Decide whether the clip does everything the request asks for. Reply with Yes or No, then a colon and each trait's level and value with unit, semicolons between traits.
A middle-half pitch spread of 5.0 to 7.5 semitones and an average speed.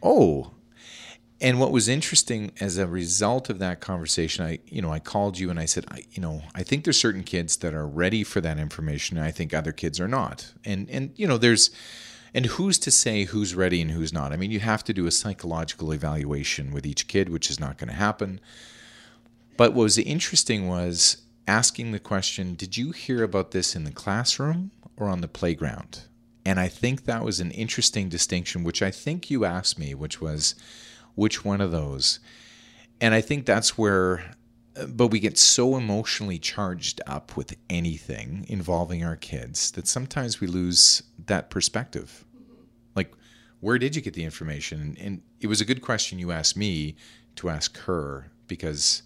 Yes: wide, 5.5 semitones; average, 190 wpm